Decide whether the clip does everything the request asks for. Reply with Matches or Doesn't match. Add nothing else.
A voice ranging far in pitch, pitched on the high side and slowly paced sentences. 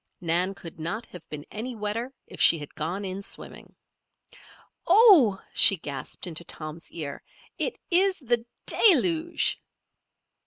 Matches